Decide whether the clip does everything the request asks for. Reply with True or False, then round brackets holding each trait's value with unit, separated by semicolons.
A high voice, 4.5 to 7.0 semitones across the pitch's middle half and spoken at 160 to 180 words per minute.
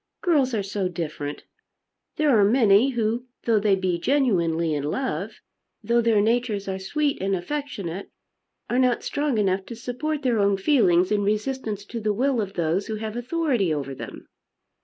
True (215 Hz; 4.8 semitones; 170 wpm)